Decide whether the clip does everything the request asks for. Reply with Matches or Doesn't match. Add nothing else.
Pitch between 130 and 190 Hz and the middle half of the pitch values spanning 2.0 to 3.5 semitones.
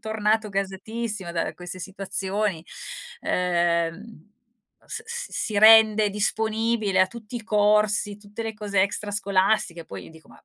Doesn't match